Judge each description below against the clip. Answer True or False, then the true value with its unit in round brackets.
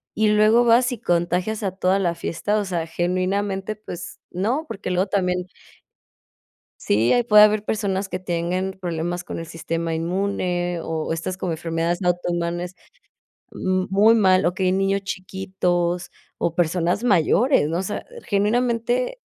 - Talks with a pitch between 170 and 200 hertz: True (185 Hz)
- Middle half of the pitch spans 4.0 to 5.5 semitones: False (2.9 semitones)